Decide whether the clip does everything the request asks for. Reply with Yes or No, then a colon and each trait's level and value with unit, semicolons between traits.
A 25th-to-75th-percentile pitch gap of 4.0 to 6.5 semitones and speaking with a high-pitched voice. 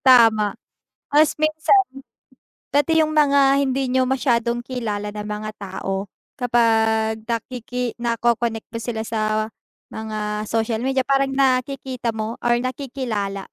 No: average, 3.3 semitones; high, 235 Hz